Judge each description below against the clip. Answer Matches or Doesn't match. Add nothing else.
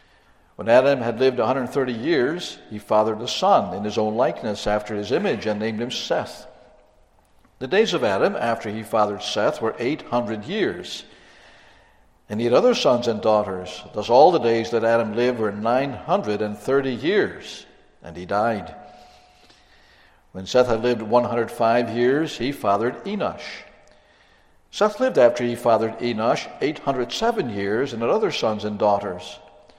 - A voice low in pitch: Matches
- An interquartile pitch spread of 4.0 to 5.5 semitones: Doesn't match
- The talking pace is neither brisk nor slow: Matches